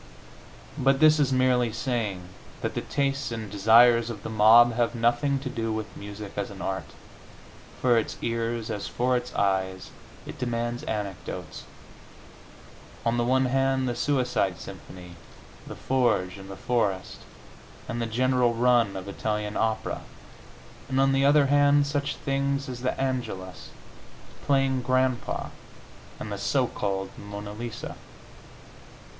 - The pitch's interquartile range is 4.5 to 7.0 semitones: No, average, 4.1 semitones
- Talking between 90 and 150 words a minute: Yes, average, 140 wpm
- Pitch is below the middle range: Yes, low, 120 Hz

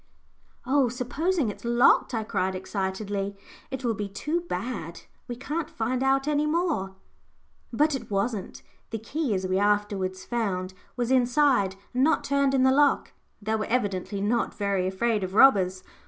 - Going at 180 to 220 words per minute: No, average, 160 wpm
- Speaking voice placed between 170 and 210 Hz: No, high, 230 Hz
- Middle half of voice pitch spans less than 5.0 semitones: No, wide, 5.4 semitones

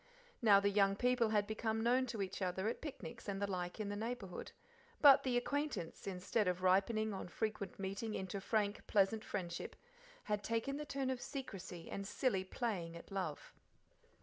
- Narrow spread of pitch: No, average, 3.4 semitones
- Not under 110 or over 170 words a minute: No, average, 180 wpm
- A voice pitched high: Yes, high, 205 Hz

